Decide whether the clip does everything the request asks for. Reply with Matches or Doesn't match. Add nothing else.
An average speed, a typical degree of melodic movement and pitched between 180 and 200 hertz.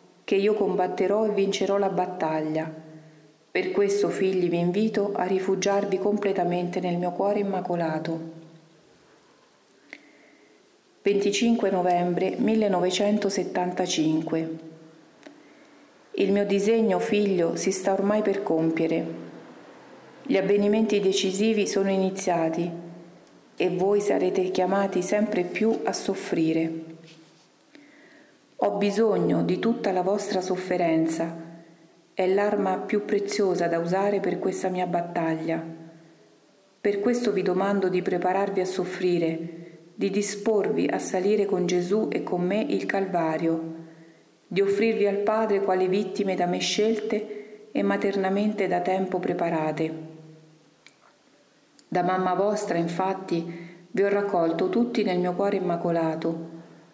Doesn't match